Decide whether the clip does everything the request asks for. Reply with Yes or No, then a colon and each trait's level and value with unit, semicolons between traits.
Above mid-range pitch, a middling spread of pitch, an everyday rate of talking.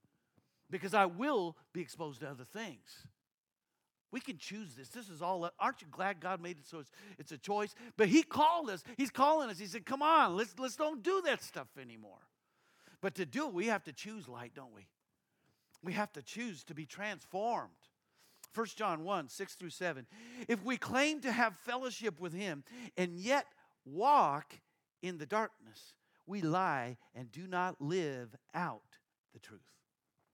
No: high, 195 Hz; wide, 6.7 semitones; average, 180 wpm